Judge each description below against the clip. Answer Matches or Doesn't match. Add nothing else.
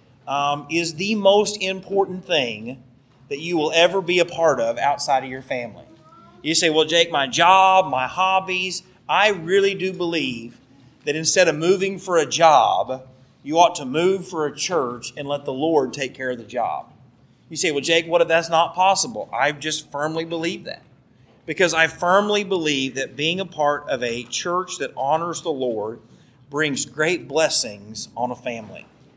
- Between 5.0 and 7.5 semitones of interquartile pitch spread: Matches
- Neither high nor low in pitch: Matches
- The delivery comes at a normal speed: Matches